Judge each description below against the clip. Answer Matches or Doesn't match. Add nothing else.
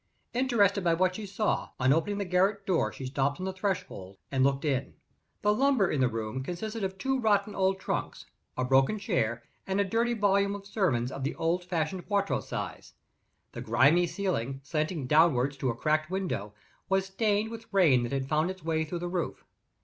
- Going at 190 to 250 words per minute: Matches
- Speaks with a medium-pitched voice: Matches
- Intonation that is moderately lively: Doesn't match